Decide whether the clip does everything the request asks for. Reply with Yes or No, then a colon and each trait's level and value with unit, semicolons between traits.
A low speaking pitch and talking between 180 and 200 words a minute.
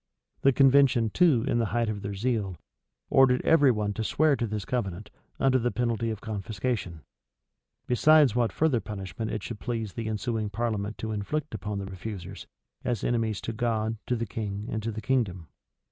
Yes: low, 110 Hz; average, 185 wpm